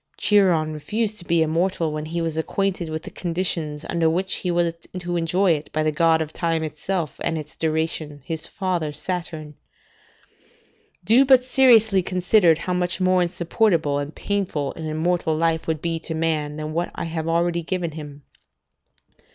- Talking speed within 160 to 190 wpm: Yes, average, 170 wpm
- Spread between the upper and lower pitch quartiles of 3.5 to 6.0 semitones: No, narrow, 2.6 semitones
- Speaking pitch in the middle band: Yes, medium, 165 Hz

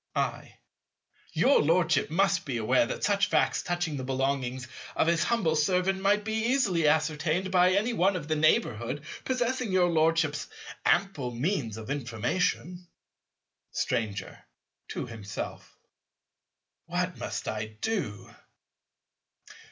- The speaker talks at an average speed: No, slow, 120 wpm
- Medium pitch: Yes, medium, 160 Hz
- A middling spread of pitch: No, wide, 6.6 semitones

